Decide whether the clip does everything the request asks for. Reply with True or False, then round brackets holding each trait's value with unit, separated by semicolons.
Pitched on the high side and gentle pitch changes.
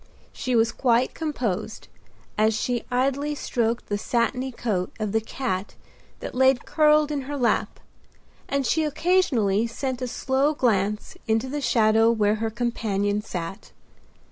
False (235 Hz; 3.7 semitones)